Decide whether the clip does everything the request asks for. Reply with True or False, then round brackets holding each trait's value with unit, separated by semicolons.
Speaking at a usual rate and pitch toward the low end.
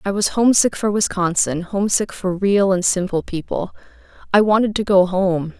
False (170 wpm; 195 Hz)